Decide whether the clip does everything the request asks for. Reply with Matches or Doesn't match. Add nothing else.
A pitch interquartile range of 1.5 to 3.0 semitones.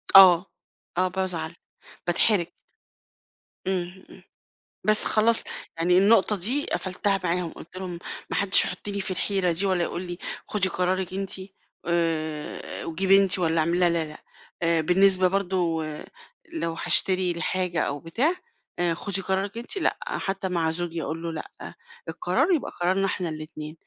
Matches